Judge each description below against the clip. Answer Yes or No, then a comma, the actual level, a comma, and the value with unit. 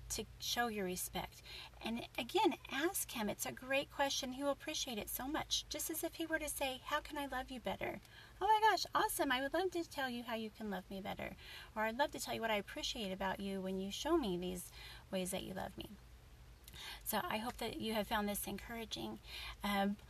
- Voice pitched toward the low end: No, high, 240 Hz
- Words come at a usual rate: No, fast, 235 wpm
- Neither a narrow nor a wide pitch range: No, wide, 7.3 semitones